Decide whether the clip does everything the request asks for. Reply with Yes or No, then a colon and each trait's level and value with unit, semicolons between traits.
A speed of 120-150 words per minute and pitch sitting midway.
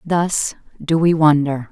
Yes: average, 140 wpm; medium, 155 Hz